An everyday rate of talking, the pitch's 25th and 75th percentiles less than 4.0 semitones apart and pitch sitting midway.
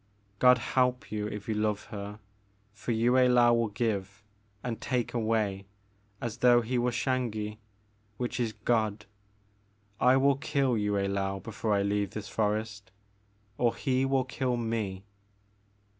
No: average, 150 wpm; average, 3.1 semitones; low, 110 Hz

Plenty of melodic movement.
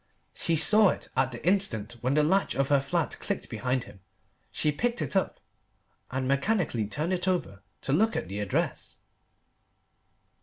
Yes: wide, 6.8 semitones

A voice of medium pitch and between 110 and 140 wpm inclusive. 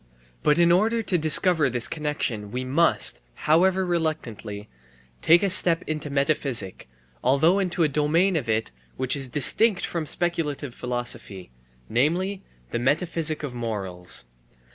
Yes: medium, 150 Hz; slow, 135 wpm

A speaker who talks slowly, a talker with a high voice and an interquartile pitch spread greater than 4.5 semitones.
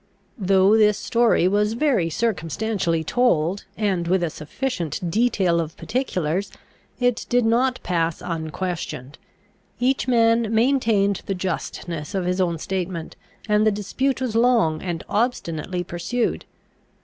Yes: slow, 125 wpm; high, 195 Hz; average, 5.2 semitones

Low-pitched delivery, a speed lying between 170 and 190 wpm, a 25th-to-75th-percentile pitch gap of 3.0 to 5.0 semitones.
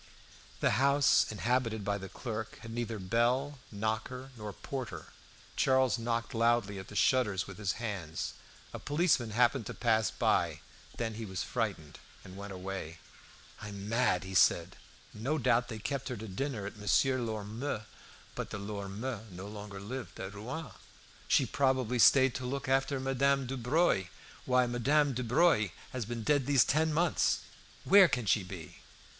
No: low, 115 Hz; average, 160 wpm; average, 4.3 semitones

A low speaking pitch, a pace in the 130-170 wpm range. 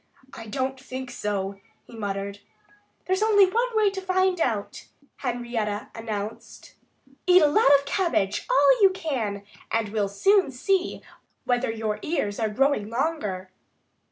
No: high, 245 Hz; average, 140 wpm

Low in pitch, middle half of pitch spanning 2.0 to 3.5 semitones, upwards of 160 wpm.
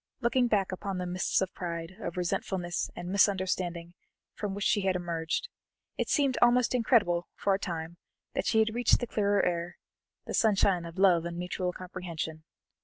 No: medium, 185 Hz; average, 2.9 semitones; average, 175 wpm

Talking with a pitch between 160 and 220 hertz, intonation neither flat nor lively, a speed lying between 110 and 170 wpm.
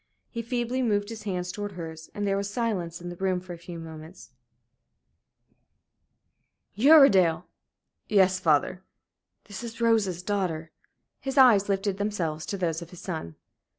Yes: high, 190 Hz; average, 3.7 semitones; average, 150 wpm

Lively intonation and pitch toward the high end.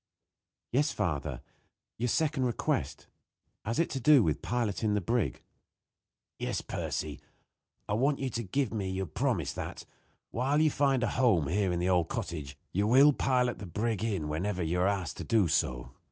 No: wide, 6.1 semitones; low, 105 Hz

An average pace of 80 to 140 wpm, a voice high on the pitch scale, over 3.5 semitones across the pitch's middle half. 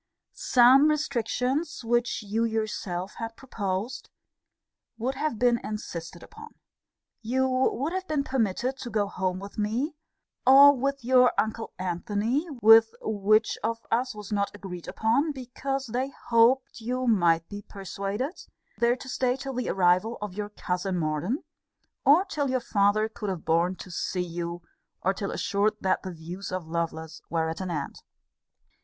No: average, 155 wpm; high, 220 Hz; average, 5.3 semitones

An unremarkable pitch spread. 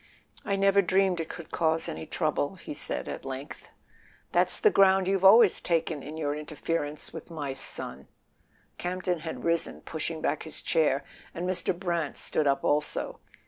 Yes: average, 3.5 semitones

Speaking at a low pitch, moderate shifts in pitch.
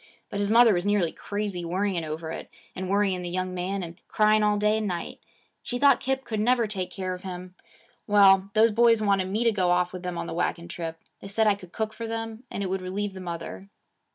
No: high, 195 Hz; average, 3.0 semitones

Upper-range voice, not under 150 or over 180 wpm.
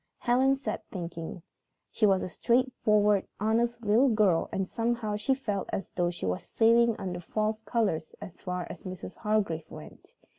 Yes: high, 210 Hz; average, 160 wpm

